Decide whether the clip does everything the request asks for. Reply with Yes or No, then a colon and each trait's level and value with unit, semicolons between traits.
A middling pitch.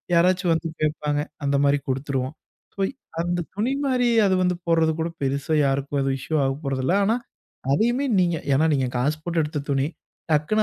Yes: medium, 155 Hz